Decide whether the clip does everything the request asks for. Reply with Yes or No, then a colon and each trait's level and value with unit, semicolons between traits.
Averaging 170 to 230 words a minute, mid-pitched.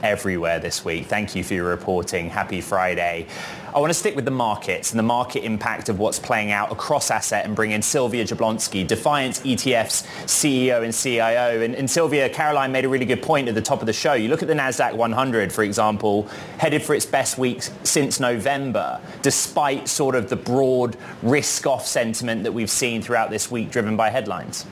No: average, 200 wpm; low, 115 Hz